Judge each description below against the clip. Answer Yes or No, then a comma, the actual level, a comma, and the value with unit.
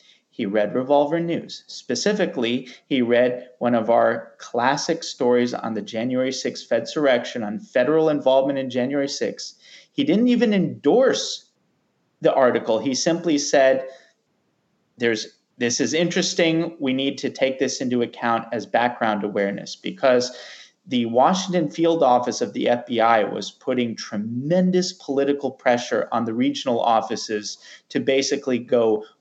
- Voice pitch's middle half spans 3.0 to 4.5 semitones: No, wide, 5.5 semitones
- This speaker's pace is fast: No, average, 140 wpm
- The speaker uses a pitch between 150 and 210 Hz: No, low, 135 Hz